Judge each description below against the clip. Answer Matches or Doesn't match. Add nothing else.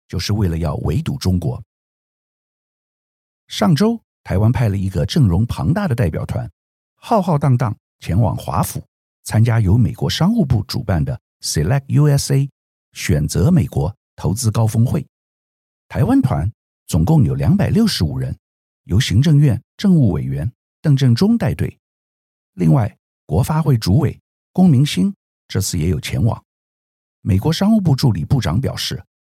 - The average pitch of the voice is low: Matches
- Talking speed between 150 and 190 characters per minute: Doesn't match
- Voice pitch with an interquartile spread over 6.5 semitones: Matches